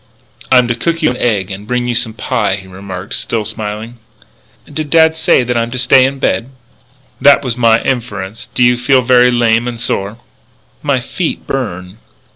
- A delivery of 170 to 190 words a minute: Yes, average, 185 wpm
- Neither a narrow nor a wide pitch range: Yes, average, 3.0 semitones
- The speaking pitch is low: Yes, low, 120 Hz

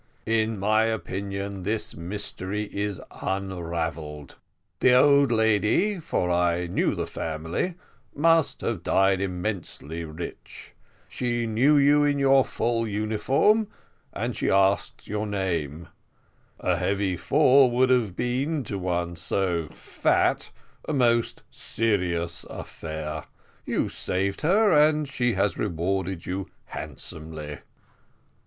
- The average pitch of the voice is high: No, low, 100 Hz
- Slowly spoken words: Yes, slow, 115 wpm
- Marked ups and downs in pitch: Yes, wide, 5.9 semitones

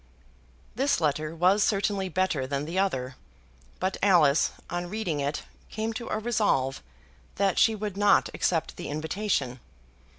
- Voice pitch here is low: No, medium, 185 Hz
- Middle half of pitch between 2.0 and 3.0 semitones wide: No, wide, 5.5 semitones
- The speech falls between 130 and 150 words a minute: Yes, average, 140 wpm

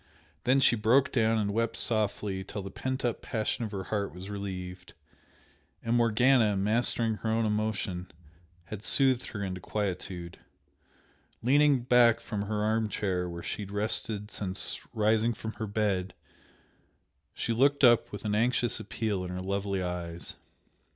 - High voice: No, low, 105 Hz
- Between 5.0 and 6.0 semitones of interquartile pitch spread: No, average, 3.0 semitones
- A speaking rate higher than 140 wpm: Yes, average, 155 wpm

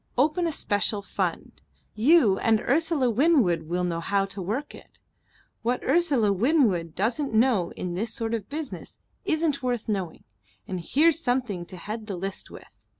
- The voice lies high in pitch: Yes, high, 225 Hz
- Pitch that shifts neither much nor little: No, wide, 6.4 semitones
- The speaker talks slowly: No, average, 160 wpm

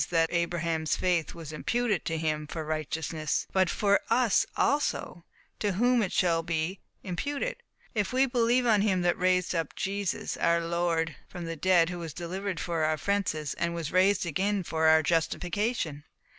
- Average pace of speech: Yes, average, 170 wpm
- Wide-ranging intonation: No, average, 3.7 semitones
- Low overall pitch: No, medium, 175 Hz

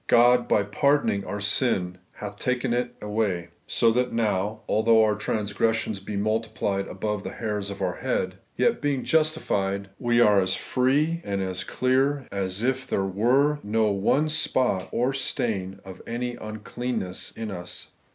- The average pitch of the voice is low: Yes, low, 110 Hz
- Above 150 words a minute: Yes, average, 160 wpm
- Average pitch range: Yes, average, 3.9 semitones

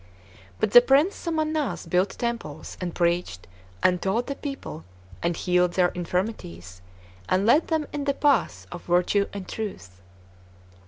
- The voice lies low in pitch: No, high, 190 Hz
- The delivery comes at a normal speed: Yes, average, 145 wpm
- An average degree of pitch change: No, wide, 7.9 semitones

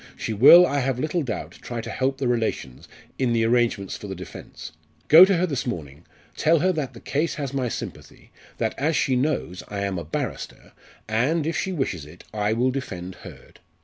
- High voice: No, low, 125 Hz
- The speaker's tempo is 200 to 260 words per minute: Yes, fast, 205 wpm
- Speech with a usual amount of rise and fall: No, wide, 6.1 semitones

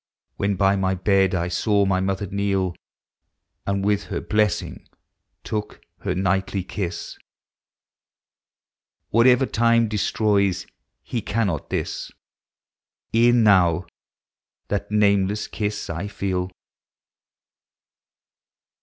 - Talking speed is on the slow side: Yes, slow, 95 wpm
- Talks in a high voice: No, low, 100 Hz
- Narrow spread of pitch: Yes, narrow, 1.9 semitones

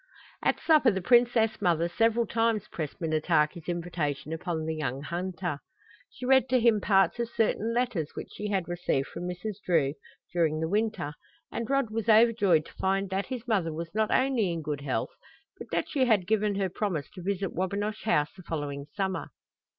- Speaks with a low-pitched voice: No, high, 190 Hz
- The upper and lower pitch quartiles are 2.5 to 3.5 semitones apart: No, average, 5.3 semitones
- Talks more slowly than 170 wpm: No, average, 185 wpm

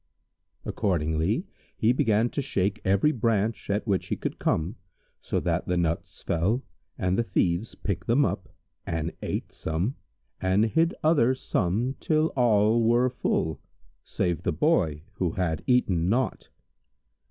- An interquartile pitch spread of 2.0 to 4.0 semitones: No, wide, 5.6 semitones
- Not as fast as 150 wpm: Yes, average, 140 wpm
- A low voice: Yes, low, 105 Hz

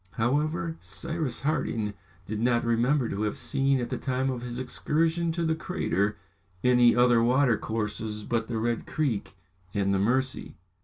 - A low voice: Yes, low, 125 Hz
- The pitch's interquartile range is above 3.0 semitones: Yes, average, 4.3 semitones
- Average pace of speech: Yes, average, 155 wpm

